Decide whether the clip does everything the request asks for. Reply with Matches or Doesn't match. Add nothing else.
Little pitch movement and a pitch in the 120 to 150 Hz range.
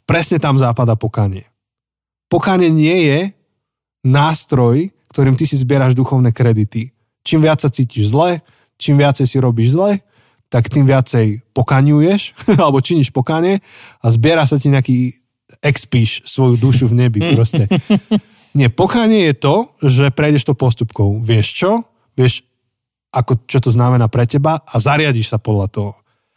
Doesn't match